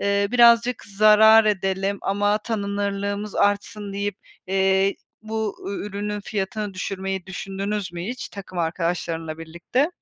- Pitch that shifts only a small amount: Yes, narrow, 1.6 semitones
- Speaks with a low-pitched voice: No, high, 200 Hz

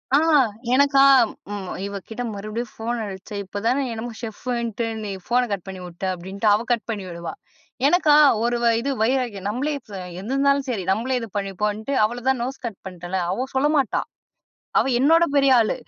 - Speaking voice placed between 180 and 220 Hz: No, high, 230 Hz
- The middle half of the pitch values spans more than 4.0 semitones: Yes, average, 4.6 semitones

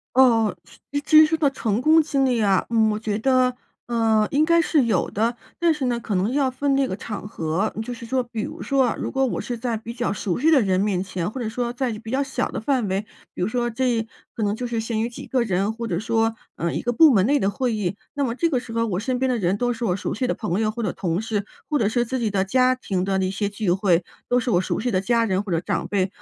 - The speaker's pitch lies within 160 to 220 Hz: No, high, 230 Hz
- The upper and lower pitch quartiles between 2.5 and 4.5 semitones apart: Yes, average, 3.9 semitones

